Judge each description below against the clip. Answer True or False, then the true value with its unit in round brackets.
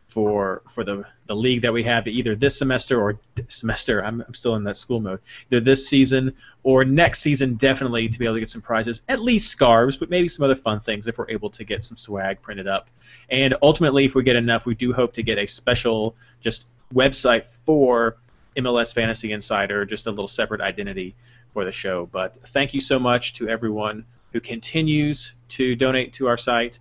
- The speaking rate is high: True (210 wpm)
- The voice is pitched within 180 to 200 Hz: False (120 Hz)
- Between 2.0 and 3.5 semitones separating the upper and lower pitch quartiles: True (3.0 semitones)